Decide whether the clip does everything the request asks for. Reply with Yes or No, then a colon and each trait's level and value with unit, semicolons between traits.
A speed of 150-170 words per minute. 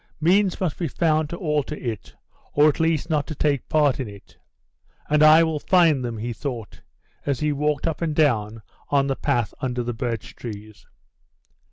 No: average, 180 wpm